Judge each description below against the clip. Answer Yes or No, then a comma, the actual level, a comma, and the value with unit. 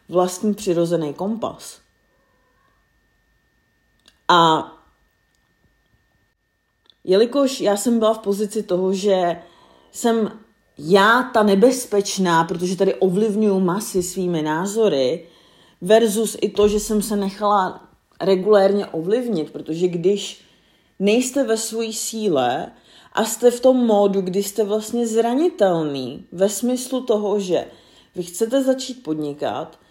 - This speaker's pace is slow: Yes, slow, 110 wpm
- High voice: Yes, high, 200 Hz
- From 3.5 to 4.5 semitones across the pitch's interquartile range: Yes, average, 3.8 semitones